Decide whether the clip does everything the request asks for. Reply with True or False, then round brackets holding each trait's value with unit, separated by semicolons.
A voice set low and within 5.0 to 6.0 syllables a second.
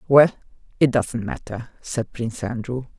False (120 Hz; 4.5 syllables/s)